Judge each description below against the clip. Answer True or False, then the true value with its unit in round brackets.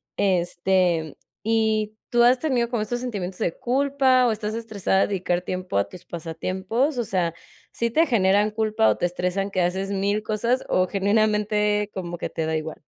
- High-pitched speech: True (205 Hz)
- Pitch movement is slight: False (3.8 semitones)